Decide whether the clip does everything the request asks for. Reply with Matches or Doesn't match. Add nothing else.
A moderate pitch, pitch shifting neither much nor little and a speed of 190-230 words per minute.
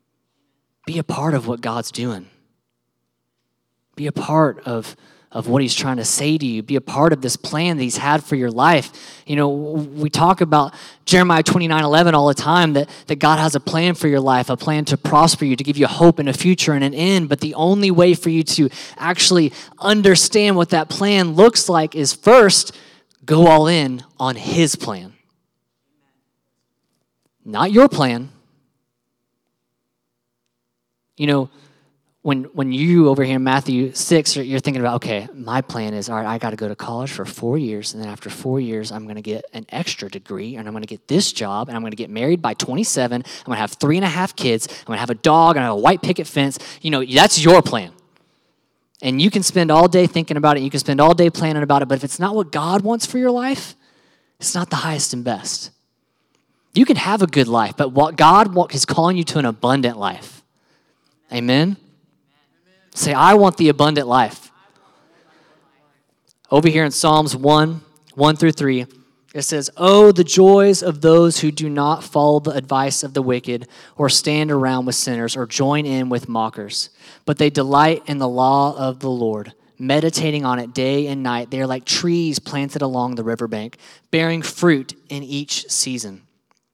Matches